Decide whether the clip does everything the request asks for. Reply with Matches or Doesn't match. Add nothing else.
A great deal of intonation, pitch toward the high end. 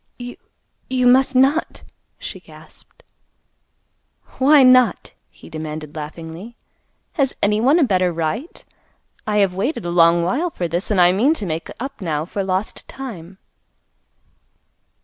Matches